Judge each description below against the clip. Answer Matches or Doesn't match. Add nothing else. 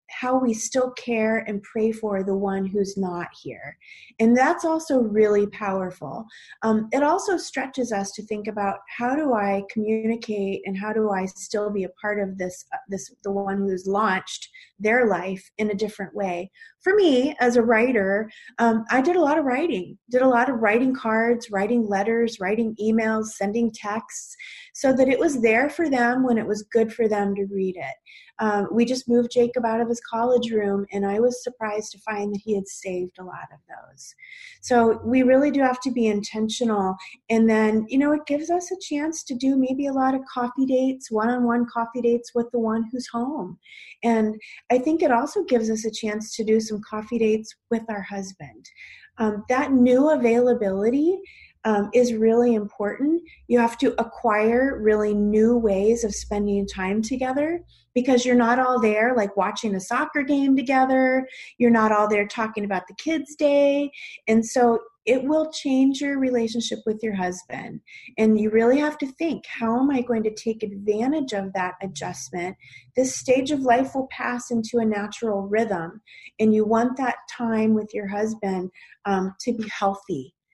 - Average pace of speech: Matches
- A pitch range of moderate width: Matches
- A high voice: Matches